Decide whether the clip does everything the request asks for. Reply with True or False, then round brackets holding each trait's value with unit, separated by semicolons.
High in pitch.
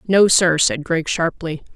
False (170 Hz)